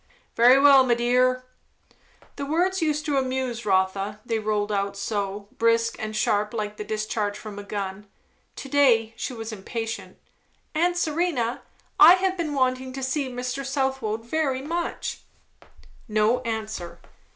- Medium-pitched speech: No, high, 240 Hz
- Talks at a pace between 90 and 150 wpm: Yes, average, 145 wpm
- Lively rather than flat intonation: No, average, 4.2 semitones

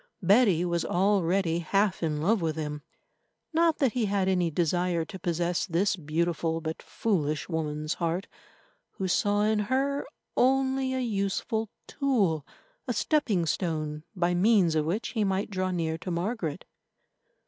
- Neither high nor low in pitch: Yes, medium, 180 Hz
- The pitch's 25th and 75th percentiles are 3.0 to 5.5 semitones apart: Yes, average, 4.3 semitones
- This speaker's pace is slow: No, average, 150 wpm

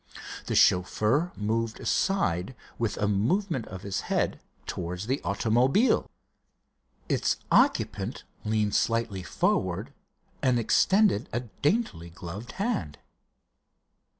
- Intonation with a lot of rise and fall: Yes, wide, 6.3 semitones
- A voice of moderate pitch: No, low, 110 Hz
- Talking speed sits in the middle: No, slow, 100 wpm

